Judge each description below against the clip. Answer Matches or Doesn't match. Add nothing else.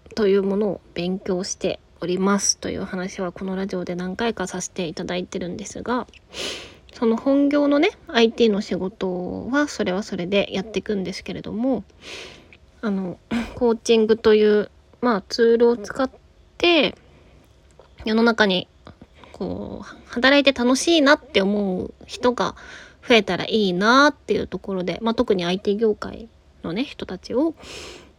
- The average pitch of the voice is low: Doesn't match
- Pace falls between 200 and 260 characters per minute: Doesn't match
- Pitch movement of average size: Matches